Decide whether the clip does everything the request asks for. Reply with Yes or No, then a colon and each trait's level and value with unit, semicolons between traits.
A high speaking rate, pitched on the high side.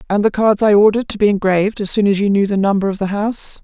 Yes: fast, 295 wpm; high, 205 Hz